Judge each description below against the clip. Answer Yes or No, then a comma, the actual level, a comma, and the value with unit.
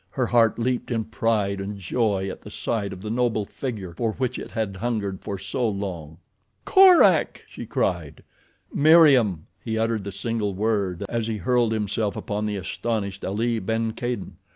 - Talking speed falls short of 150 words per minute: No, average, 170 wpm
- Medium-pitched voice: No, low, 110 Hz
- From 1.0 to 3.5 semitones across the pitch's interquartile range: Yes, average, 2.9 semitones